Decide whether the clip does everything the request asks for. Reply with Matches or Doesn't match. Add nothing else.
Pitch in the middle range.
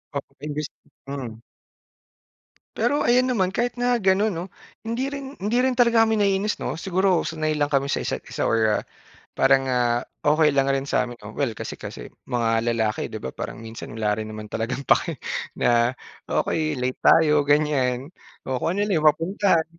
Matches